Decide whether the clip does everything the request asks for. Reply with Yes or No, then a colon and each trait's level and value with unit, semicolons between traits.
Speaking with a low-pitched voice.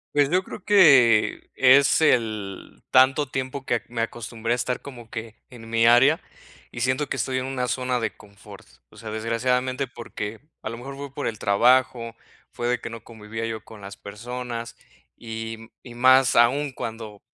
Yes: low, 120 Hz